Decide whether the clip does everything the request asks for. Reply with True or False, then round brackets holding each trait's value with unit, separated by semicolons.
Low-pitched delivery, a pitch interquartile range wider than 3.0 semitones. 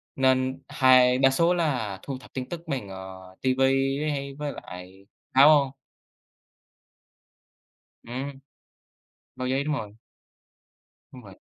False (130 Hz; 2.7 semitones)